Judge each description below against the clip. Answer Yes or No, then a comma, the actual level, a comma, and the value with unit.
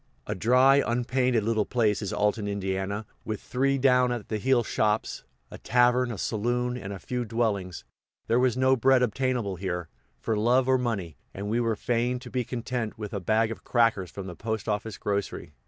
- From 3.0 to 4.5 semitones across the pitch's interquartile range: Yes, average, 3.4 semitones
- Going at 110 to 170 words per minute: No, average, 190 wpm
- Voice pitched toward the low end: Yes, low, 115 Hz